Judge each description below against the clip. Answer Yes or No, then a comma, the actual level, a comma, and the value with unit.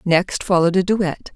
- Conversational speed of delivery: Yes, average, 175 wpm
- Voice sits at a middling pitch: Yes, medium, 180 Hz